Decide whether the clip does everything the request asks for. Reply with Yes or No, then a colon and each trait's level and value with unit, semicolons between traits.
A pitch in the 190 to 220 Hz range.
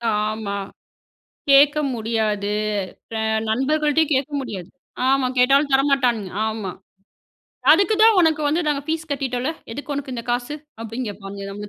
No: very high, 255 Hz